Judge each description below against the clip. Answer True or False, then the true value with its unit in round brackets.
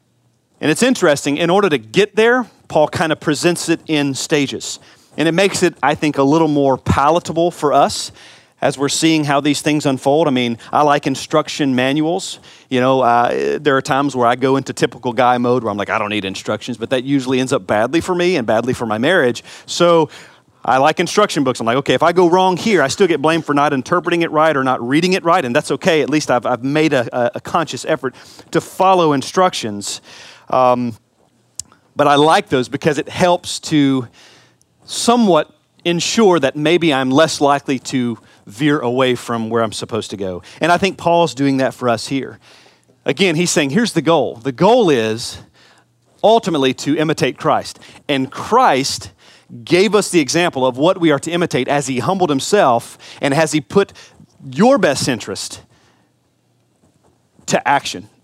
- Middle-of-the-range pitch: True (145 Hz)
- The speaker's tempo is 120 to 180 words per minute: False (195 wpm)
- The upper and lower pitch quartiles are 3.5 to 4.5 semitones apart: False (4.9 semitones)